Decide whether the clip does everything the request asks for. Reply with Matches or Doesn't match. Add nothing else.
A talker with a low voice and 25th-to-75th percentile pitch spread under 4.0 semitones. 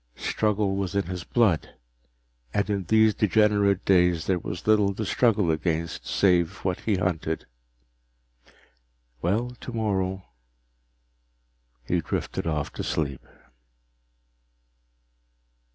Matches